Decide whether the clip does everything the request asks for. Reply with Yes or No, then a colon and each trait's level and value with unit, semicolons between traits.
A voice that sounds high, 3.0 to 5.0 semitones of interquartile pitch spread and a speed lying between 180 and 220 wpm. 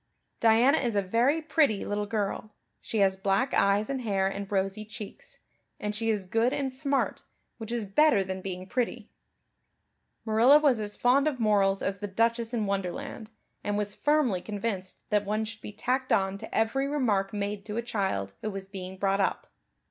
Yes: high, 210 Hz; average, 3.4 semitones; average, 185 wpm